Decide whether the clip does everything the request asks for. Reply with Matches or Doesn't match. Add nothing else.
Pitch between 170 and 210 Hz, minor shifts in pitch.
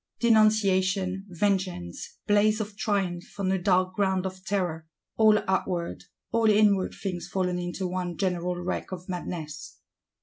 Matches